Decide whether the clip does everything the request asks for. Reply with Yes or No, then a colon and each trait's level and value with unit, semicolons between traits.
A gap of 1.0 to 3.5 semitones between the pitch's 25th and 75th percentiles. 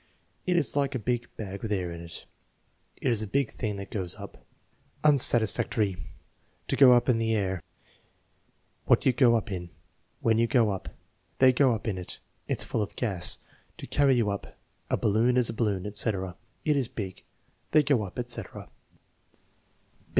No: average, 4.1 semitones